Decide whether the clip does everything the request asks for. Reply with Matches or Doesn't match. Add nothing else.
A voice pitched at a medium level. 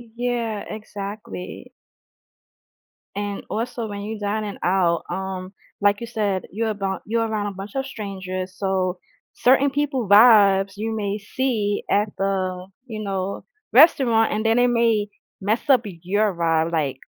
Doesn't match